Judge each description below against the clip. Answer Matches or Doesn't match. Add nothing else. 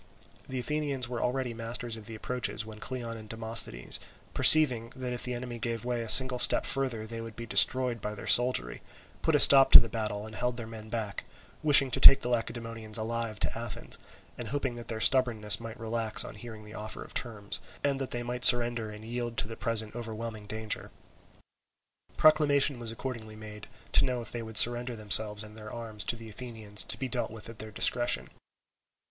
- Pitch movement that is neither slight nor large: Doesn't match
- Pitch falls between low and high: Doesn't match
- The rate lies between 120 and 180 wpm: Doesn't match